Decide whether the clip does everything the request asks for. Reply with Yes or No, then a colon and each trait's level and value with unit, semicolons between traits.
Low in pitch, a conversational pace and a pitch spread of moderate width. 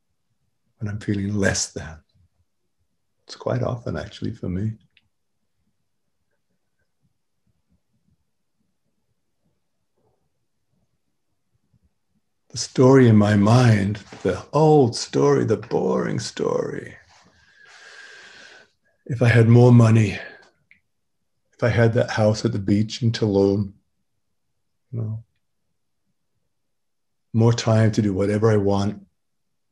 No: low, 110 Hz; slow, 95 wpm; average, 3.1 semitones